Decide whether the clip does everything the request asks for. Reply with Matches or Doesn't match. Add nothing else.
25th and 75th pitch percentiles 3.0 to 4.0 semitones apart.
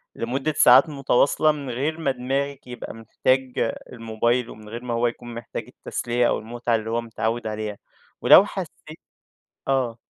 Doesn't match